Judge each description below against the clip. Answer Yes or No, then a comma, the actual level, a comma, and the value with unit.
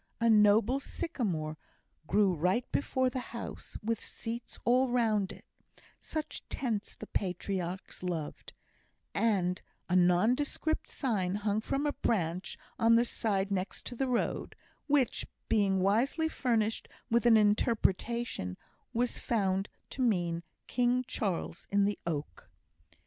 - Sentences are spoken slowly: Yes, slow, 125 wpm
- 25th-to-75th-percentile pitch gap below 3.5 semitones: No, average, 4.3 semitones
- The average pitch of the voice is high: Yes, high, 215 Hz